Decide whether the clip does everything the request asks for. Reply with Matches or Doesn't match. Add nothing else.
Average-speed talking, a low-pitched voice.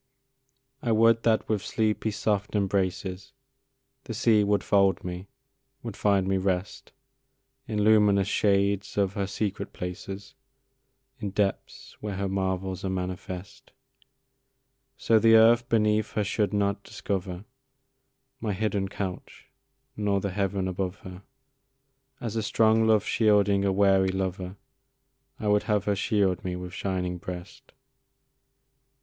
Doesn't match